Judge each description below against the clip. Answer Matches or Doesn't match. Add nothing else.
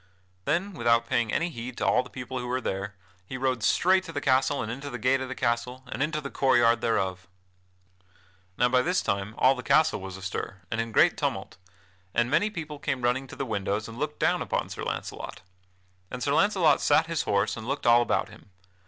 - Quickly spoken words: Matches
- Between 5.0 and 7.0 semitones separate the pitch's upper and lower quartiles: Doesn't match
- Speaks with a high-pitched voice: Doesn't match